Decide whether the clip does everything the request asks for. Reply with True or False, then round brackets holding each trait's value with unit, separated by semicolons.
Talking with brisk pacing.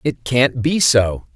False (175 wpm)